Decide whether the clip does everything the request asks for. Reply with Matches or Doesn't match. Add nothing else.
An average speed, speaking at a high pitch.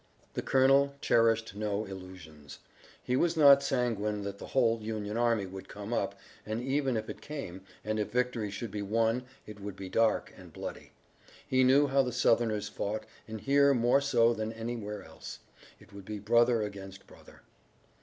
Doesn't match